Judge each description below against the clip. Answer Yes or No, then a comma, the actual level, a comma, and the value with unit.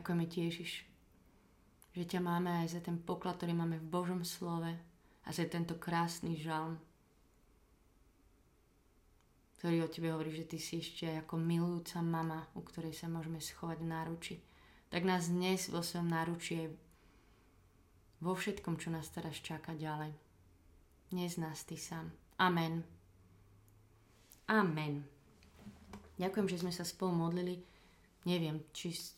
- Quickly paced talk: No, average, 135 wpm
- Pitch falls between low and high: Yes, medium, 165 Hz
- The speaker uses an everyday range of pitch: No, narrow, 2.2 semitones